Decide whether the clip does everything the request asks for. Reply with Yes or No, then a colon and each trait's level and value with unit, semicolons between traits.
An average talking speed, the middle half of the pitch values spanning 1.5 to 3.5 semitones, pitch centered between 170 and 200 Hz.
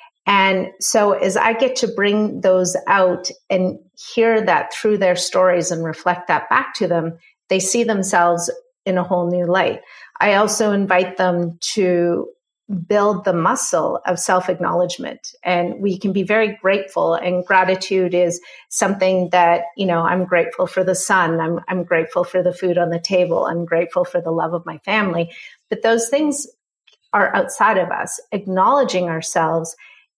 Yes: average, 165 wpm; average, 2.9 semitones; medium, 185 Hz